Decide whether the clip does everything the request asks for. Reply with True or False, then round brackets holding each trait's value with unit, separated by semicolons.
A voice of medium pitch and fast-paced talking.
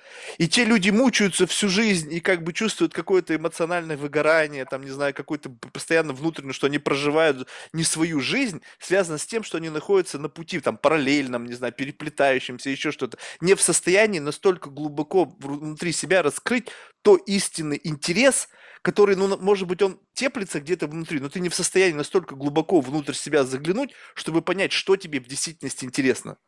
True (165 Hz; 170 wpm)